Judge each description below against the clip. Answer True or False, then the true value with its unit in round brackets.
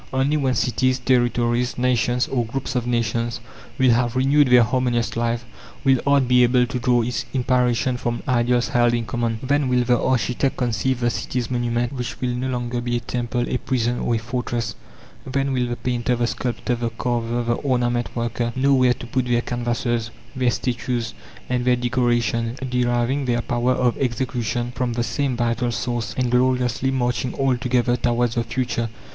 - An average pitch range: False (1.2 semitones)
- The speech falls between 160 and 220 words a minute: True (180 wpm)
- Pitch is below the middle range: True (120 Hz)